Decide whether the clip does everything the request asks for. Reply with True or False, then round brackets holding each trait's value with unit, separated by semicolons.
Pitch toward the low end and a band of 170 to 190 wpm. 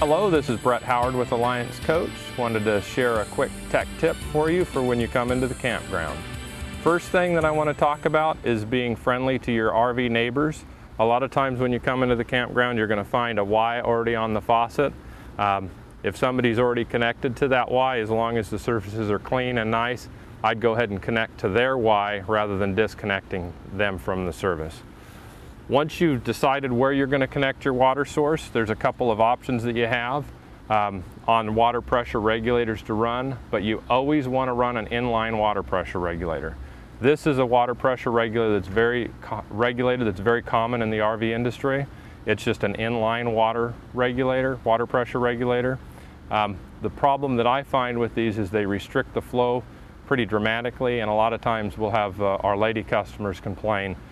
False (120 Hz; 200 wpm)